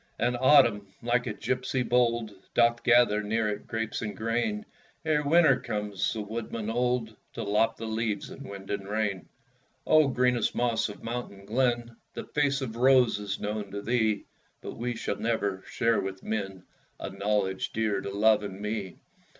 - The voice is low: Yes, low, 110 Hz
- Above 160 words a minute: Yes, average, 170 wpm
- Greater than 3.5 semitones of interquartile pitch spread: No, average, 2.9 semitones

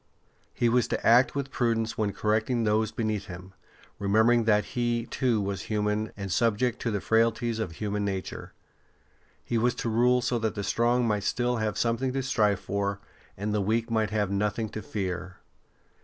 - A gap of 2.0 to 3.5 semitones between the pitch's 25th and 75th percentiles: Yes, narrow, 2.4 semitones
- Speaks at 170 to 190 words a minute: Yes, average, 180 wpm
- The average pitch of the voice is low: Yes, low, 110 Hz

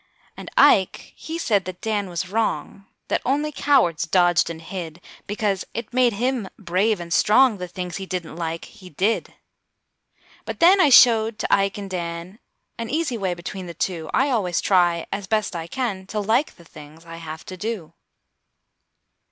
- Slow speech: No, average, 175 wpm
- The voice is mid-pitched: No, high, 195 Hz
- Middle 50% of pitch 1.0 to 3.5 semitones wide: No, average, 4.6 semitones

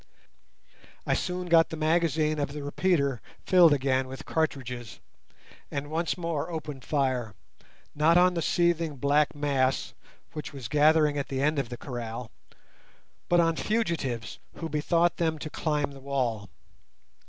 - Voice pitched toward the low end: No, medium, 150 Hz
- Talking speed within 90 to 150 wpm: Yes, average, 145 wpm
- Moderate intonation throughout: Yes, average, 3.6 semitones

